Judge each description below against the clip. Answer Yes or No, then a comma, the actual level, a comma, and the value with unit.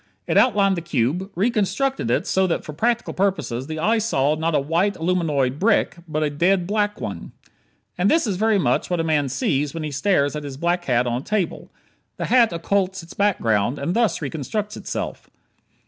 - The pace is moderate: Yes, average, 195 wpm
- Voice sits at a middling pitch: Yes, medium, 170 Hz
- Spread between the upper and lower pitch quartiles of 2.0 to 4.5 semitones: No, wide, 5.6 semitones